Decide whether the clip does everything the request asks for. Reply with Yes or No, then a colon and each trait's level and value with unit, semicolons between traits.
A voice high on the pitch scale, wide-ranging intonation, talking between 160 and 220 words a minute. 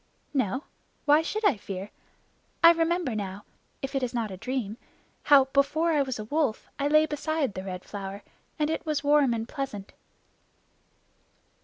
Yes: very high, 270 Hz; wide, 6.4 semitones; average, 165 wpm